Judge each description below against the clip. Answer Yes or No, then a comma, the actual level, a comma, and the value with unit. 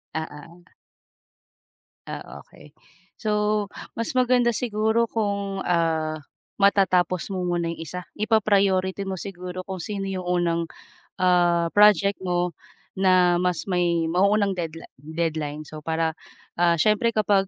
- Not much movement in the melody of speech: No, average, 3.1 semitones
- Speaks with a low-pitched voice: No, medium, 185 Hz